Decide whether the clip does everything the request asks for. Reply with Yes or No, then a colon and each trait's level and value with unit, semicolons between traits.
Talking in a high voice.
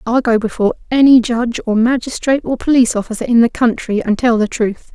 Yes: high, 235 Hz